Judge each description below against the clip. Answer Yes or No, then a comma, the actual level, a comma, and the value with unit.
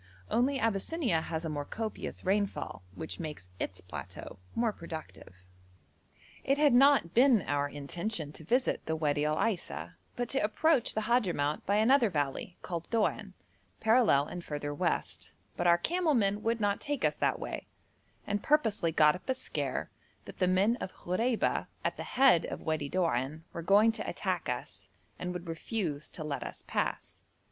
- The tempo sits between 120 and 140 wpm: No, average, 170 wpm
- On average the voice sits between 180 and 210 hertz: Yes, medium, 185 Hz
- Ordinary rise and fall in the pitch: No, wide, 6.9 semitones